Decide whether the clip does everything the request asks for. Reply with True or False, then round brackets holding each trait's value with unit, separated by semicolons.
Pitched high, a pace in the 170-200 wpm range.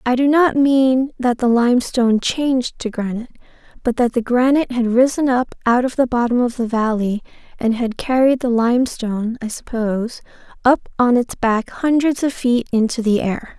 True (245 Hz; 180 wpm)